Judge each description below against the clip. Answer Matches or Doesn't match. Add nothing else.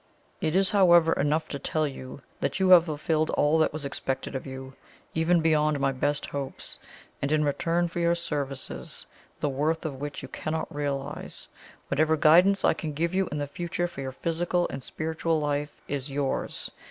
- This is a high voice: Doesn't match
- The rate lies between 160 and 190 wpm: Matches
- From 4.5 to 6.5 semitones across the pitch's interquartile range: Doesn't match